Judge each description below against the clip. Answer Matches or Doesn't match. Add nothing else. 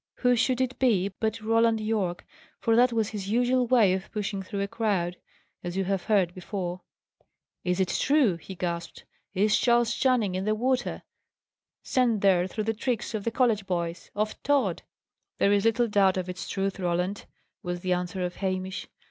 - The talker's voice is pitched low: Doesn't match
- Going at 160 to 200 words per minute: Matches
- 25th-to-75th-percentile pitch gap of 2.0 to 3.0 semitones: Doesn't match